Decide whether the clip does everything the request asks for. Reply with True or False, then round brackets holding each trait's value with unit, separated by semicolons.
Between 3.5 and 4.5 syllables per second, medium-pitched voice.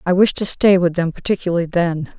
False (5.9 syllables/s; 180 Hz)